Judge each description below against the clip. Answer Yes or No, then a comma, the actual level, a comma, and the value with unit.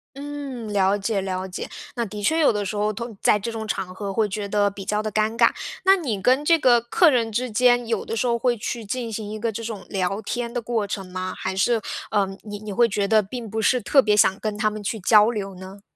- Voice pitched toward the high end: Yes, high, 215 Hz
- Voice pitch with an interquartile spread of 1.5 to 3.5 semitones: Yes, average, 2.8 semitones